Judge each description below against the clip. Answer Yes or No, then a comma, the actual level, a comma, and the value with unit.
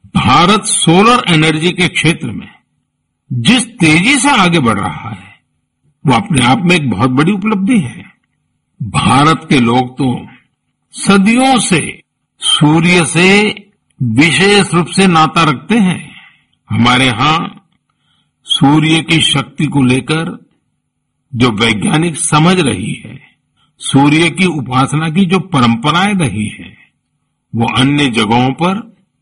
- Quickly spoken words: No, average, 125 wpm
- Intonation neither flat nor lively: No, wide, 6.0 semitones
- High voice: No, medium, 160 Hz